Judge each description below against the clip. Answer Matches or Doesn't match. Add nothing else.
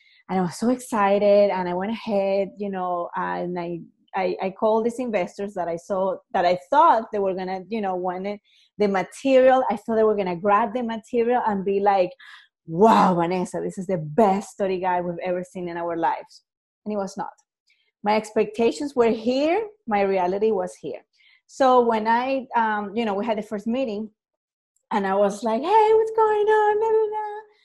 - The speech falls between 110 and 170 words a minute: Doesn't match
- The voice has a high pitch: Matches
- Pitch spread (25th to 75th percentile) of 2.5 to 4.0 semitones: Doesn't match